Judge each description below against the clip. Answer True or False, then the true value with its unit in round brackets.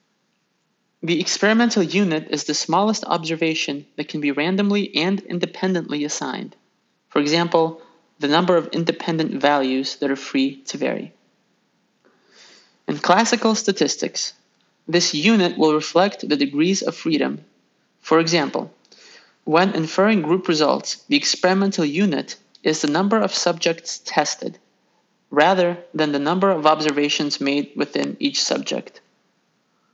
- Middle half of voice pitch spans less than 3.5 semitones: False (4.3 semitones)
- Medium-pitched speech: True (170 Hz)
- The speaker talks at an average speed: False (125 wpm)